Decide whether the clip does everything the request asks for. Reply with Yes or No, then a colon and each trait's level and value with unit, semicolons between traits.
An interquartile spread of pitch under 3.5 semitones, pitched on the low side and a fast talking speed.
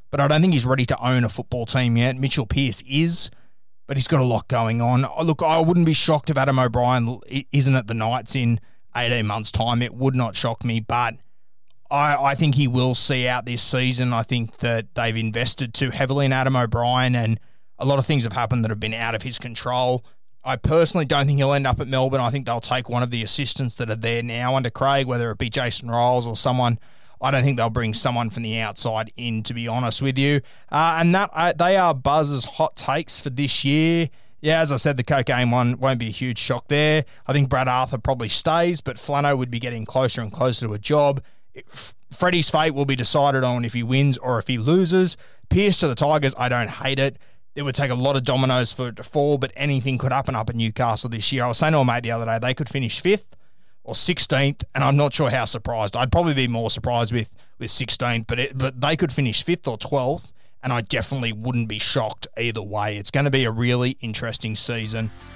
Yes: average, 3.1 semitones; low, 125 Hz; fast, 240 wpm